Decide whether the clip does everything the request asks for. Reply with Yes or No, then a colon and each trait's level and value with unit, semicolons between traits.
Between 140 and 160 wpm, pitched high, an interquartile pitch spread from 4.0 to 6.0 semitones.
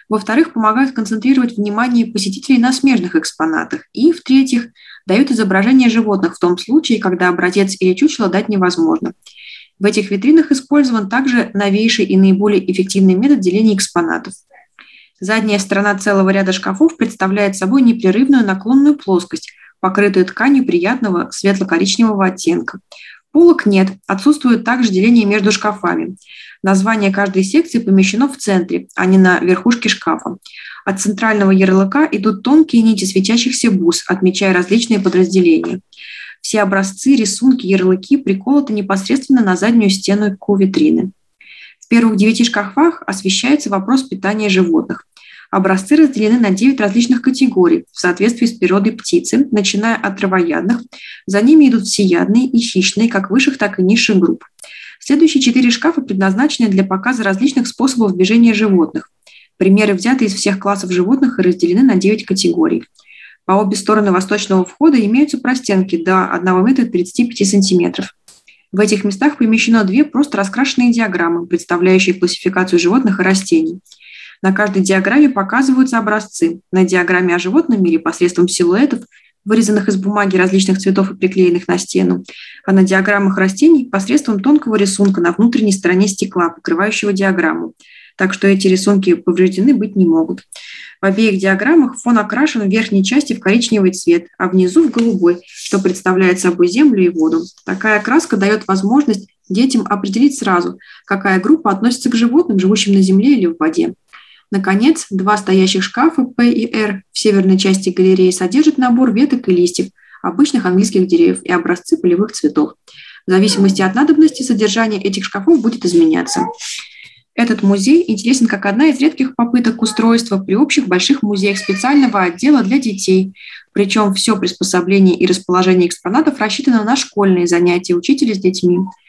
Yes: average, 145 wpm; high, 205 Hz; average, 4.8 semitones